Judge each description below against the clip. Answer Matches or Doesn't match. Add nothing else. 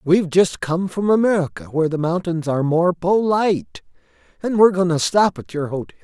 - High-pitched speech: Doesn't match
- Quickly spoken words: Doesn't match